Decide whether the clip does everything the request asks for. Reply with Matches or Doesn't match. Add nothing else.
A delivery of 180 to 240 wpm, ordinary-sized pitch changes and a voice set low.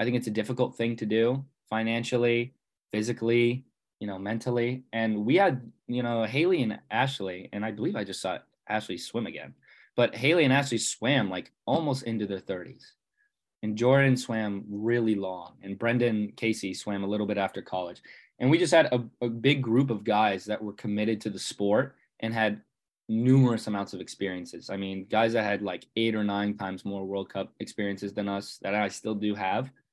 Matches